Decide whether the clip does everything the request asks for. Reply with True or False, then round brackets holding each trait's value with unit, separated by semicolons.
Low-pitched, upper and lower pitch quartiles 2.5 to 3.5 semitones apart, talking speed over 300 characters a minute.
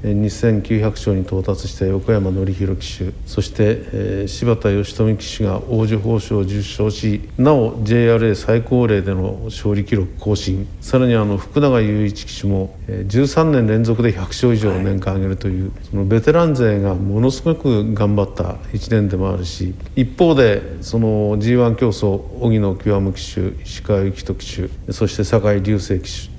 False (105 Hz; 2.9 semitones; 290 characters per minute)